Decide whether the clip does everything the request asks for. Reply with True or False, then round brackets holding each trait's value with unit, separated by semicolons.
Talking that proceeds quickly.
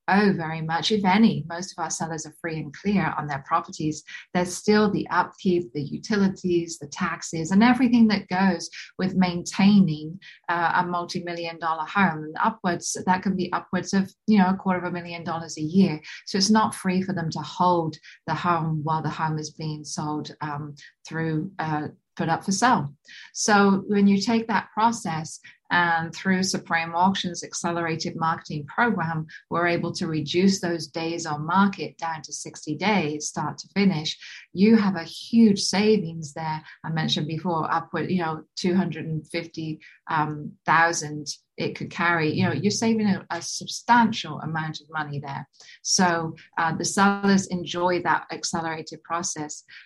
False (165 wpm)